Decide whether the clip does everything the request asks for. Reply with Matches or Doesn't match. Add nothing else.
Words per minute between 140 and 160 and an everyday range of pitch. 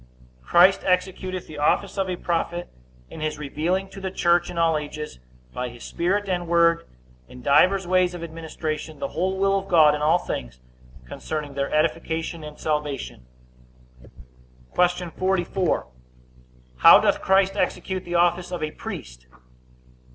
Matches